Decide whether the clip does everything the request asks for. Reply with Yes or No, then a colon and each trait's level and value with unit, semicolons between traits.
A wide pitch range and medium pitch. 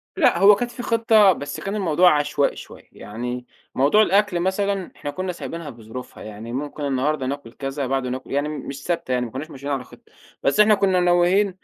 Yes: wide, 6.3 semitones; medium, 150 Hz